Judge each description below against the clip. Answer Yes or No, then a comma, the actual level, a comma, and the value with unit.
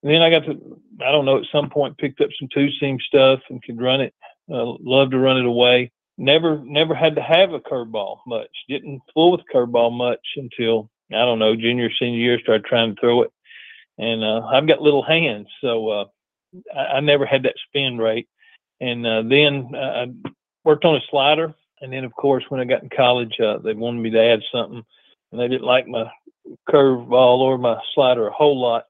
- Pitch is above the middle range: No, low, 130 Hz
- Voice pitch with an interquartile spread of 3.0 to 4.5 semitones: Yes, average, 3.8 semitones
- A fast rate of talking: Yes, fast, 215 wpm